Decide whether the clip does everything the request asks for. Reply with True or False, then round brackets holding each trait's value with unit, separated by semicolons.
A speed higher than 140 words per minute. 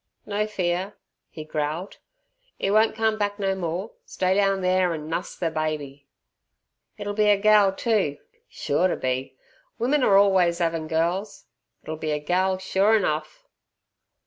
True (150 wpm)